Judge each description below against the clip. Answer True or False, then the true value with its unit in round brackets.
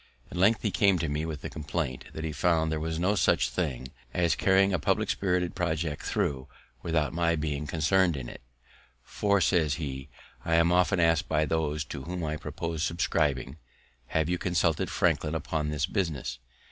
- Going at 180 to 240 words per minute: True (185 wpm)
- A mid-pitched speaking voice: False (80 Hz)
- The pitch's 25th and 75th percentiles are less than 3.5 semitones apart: True (2.8 semitones)